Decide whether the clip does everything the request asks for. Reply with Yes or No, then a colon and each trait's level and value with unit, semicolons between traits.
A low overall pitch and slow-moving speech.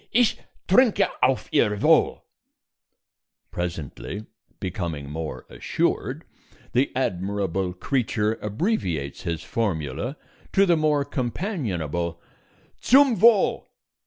Yes: low, 105 Hz; slow, 90 wpm